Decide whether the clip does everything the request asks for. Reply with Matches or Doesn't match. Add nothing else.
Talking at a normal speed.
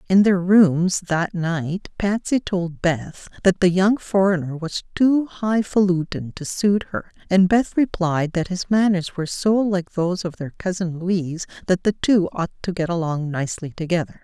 Matches